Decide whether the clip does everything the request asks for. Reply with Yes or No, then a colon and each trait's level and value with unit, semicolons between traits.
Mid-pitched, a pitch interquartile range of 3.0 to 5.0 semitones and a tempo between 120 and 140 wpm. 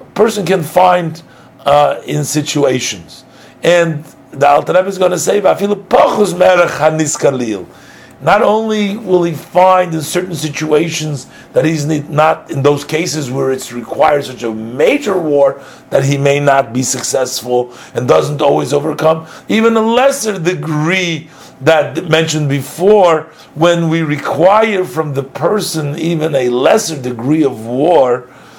Yes: medium, 155 Hz; average, 4.1 semitones; slow, 135 wpm